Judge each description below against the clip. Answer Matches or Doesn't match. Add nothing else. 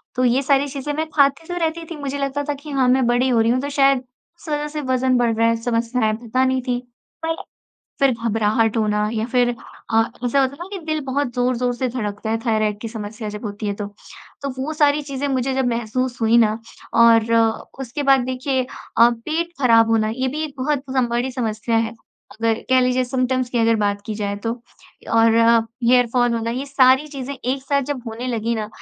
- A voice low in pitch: Doesn't match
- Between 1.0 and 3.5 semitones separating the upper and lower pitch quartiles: Matches